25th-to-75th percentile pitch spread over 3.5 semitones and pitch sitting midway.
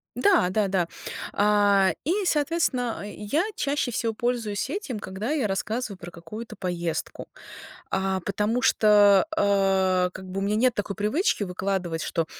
No: average, 3.9 semitones; high, 205 Hz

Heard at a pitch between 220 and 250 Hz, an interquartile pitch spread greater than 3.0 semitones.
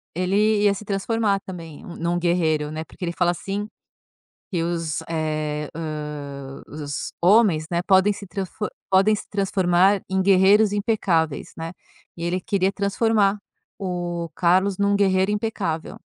No: medium, 185 Hz; average, 3.4 semitones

